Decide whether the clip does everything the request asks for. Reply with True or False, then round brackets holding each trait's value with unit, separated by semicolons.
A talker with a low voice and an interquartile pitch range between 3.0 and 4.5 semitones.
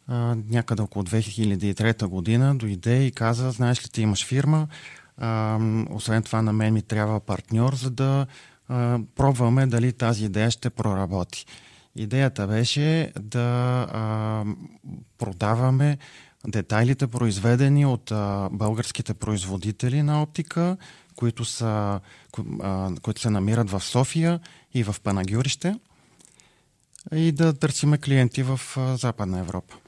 True (120 Hz; 3.8 semitones)